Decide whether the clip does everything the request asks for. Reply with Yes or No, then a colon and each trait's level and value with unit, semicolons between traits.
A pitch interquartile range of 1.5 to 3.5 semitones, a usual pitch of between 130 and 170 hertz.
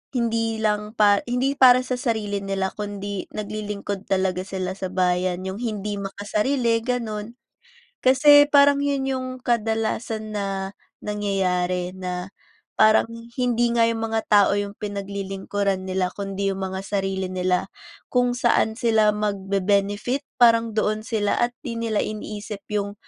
No: average, 2.9 semitones; high, 210 Hz